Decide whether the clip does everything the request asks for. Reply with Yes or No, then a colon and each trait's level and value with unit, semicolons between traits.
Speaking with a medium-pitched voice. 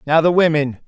Yes: medium, 155 Hz